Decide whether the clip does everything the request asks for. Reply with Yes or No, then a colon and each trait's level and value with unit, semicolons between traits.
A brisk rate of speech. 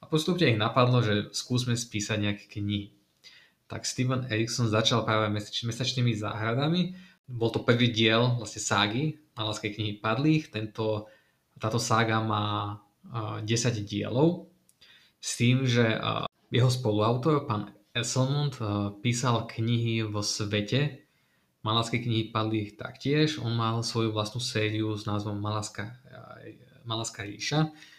No: average, 115 wpm